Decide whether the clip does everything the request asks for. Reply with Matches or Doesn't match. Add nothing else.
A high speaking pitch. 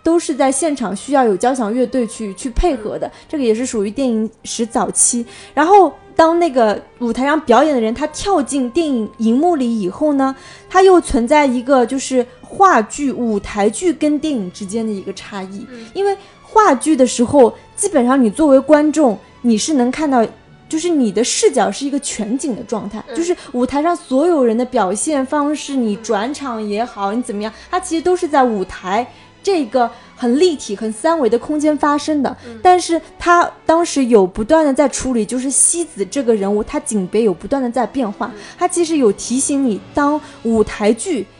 Matches